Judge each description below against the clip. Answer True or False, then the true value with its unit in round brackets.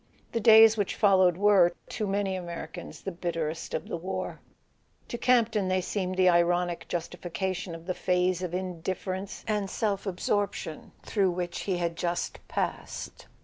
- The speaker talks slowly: False (155 wpm)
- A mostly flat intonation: True (2.3 semitones)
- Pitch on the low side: False (185 Hz)